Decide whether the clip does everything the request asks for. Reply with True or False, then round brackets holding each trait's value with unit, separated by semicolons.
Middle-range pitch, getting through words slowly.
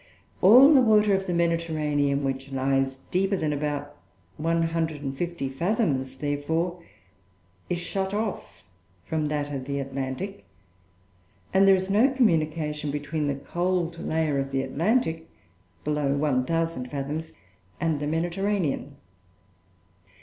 True (160 Hz; 120 wpm)